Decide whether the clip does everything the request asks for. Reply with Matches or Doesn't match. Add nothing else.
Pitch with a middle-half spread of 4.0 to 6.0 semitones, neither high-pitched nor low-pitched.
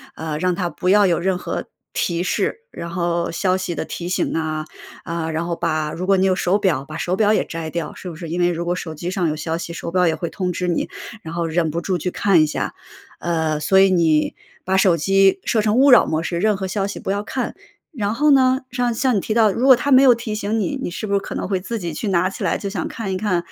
Doesn't match